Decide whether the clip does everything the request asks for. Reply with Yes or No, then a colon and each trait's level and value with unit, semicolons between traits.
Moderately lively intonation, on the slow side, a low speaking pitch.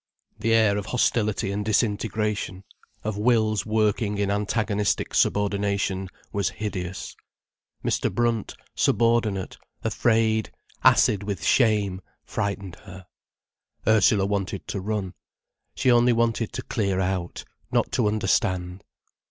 No: narrow, 2.0 semitones; slow, 110 wpm; low, 105 Hz